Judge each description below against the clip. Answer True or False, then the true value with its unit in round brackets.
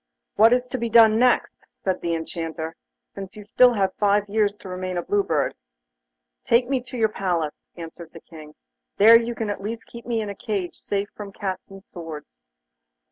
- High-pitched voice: True (200 Hz)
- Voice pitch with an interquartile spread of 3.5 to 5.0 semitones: True (4.3 semitones)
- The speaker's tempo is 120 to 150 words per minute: False (195 wpm)